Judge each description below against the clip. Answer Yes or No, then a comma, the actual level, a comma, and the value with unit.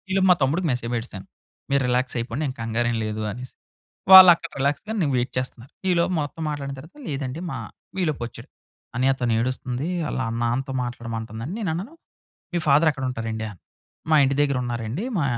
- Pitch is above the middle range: No, low, 130 Hz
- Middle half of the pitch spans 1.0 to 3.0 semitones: No, average, 4.5 semitones